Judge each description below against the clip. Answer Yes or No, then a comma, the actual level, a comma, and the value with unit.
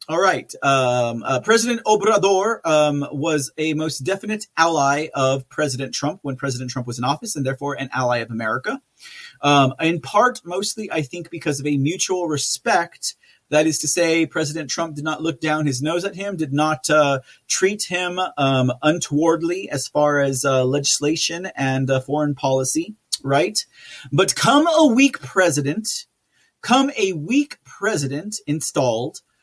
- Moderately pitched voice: Yes, medium, 155 Hz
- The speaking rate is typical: Yes, average, 160 wpm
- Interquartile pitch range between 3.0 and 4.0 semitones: No, average, 5.0 semitones